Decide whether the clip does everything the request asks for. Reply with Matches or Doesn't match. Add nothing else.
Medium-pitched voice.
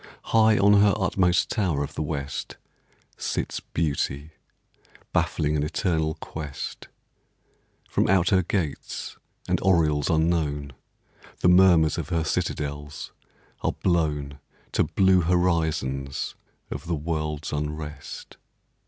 Doesn't match